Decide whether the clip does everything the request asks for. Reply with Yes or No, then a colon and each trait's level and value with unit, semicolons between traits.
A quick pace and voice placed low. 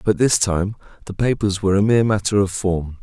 Yes: fast, 220 wpm; low, 100 Hz